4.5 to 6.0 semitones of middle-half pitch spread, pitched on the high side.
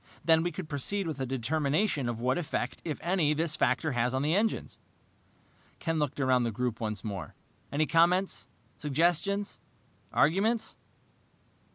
No: average, 5.1 semitones; medium, 150 Hz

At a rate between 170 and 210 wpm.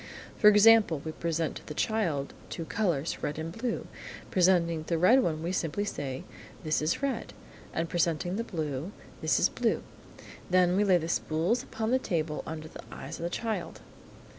Yes: average, 180 wpm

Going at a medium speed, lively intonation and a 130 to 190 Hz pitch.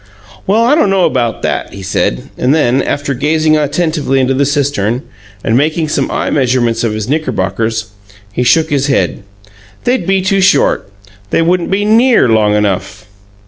Yes: average, 170 wpm; wide, 6.3 semitones; medium, 140 Hz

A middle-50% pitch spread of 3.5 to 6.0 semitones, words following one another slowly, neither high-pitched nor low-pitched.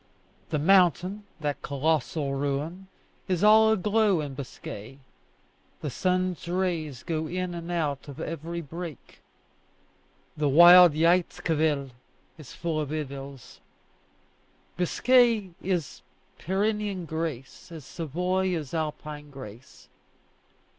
Yes: average, 4.0 semitones; slow, 105 wpm; medium, 165 Hz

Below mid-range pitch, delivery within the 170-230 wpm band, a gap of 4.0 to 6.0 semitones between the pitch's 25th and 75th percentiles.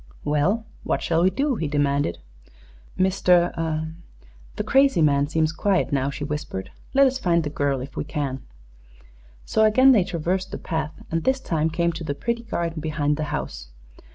No: medium, 160 Hz; average, 175 wpm; average, 4.4 semitones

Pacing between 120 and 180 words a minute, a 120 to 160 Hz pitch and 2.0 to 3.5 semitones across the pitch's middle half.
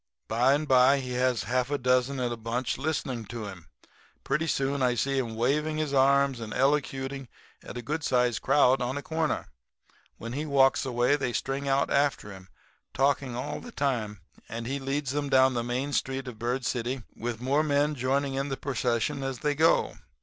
No: average, 195 wpm; low, 135 Hz; narrow, 2.4 semitones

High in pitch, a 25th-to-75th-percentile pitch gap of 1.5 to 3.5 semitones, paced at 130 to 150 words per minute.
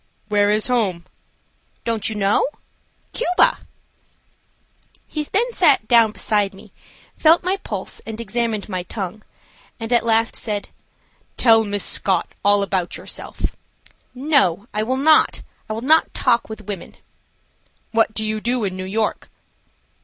Yes: high, 220 Hz; average, 3.0 semitones; average, 140 wpm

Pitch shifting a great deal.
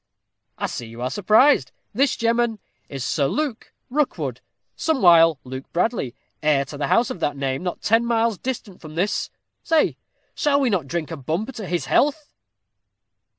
Yes: wide, 8.6 semitones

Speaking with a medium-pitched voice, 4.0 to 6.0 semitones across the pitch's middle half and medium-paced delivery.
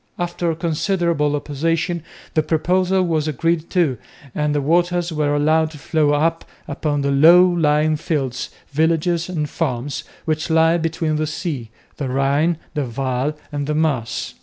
No: medium, 155 Hz; narrow, 2.4 semitones; average, 150 wpm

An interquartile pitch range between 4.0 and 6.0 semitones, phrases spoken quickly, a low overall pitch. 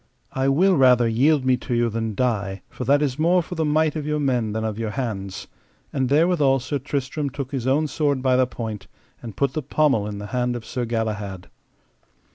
Yes: average, 4.4 semitones; fast, 215 wpm; low, 130 Hz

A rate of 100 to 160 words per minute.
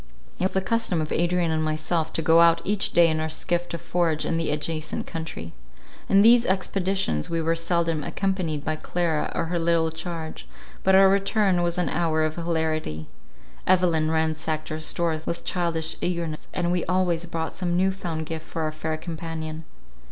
No: average, 185 wpm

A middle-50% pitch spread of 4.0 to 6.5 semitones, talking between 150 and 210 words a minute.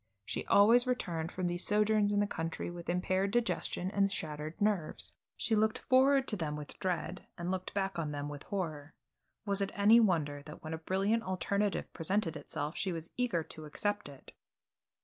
Yes: average, 4.3 semitones; average, 185 wpm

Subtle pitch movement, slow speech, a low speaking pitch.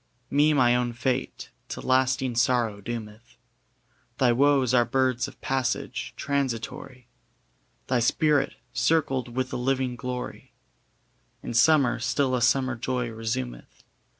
Yes: narrow, 2.0 semitones; slow, 125 wpm; low, 125 Hz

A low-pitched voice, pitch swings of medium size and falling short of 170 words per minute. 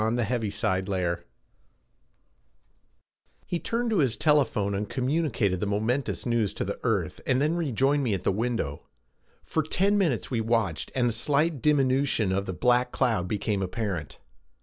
No: low, 120 Hz; wide, 5.8 semitones; average, 145 wpm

